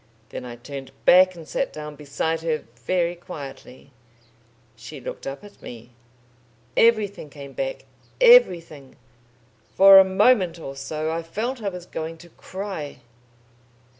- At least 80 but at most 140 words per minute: Yes, slow, 135 wpm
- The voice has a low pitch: No, medium, 165 Hz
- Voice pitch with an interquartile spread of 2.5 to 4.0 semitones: No, average, 5.2 semitones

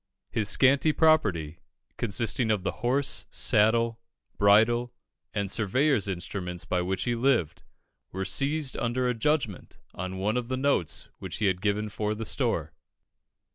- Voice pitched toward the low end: Yes, low, 110 Hz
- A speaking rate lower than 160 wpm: Yes, average, 145 wpm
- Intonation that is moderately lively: Yes, average, 4.5 semitones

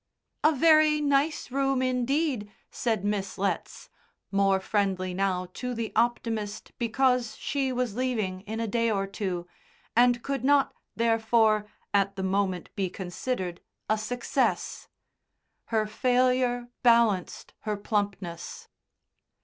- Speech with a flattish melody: No, average, 4.2 semitones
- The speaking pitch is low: No, high, 225 Hz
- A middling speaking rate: No, slow, 120 wpm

